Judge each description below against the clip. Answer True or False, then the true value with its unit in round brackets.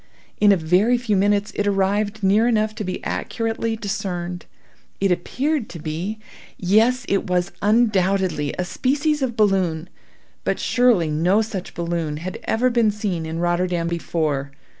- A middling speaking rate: True (145 wpm)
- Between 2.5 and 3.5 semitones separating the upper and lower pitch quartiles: False (3.9 semitones)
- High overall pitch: True (195 Hz)